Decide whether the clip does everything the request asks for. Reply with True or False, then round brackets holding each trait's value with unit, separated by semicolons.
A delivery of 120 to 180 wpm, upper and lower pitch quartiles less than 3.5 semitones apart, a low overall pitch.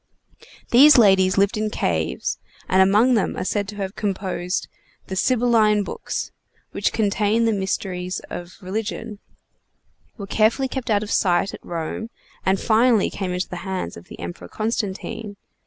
False (155 wpm; 2.8 semitones; 200 Hz)